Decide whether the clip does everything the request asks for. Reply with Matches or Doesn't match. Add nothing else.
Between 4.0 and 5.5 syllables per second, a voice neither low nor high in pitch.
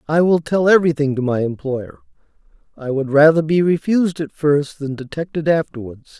Matches